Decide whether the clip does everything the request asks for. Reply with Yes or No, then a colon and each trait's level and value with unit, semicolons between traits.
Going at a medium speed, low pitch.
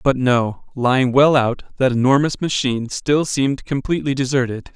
Yes: average, 150 wpm; low, 130 Hz